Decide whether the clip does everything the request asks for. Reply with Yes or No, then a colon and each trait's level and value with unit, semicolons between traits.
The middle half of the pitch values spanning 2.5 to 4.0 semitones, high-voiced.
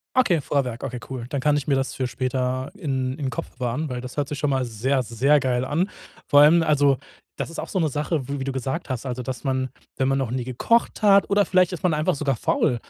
No: average, 2.8 semitones; low, 135 Hz